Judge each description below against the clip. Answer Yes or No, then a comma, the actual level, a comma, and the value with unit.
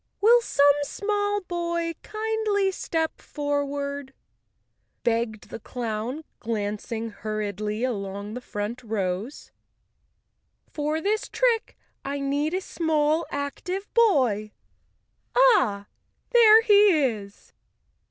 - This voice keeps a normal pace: No, slow, 95 wpm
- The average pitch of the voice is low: No, very high, 285 Hz